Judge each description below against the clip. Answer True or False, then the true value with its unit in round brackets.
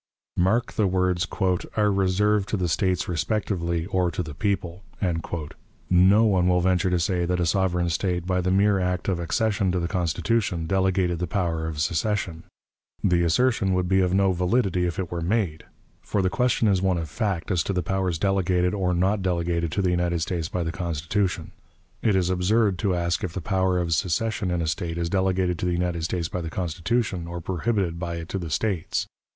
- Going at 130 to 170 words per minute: False (200 wpm)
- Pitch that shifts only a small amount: True (2.1 semitones)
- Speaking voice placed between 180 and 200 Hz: False (90 Hz)